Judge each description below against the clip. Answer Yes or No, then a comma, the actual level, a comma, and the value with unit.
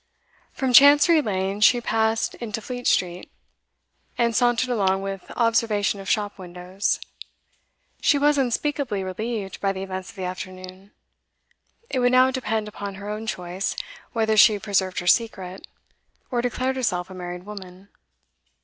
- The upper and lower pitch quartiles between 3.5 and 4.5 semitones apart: Yes, average, 4.2 semitones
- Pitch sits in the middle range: No, high, 210 Hz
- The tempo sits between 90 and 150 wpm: Yes, average, 145 wpm